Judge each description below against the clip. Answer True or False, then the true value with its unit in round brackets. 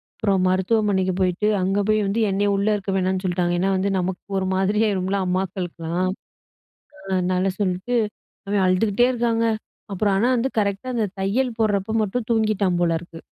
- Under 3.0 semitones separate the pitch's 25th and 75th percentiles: True (2.6 semitones)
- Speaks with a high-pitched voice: True (195 Hz)